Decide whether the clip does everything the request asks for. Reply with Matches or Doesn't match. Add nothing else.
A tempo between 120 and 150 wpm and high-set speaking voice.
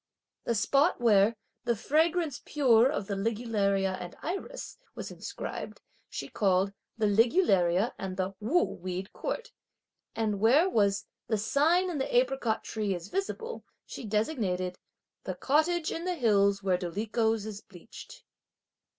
Matches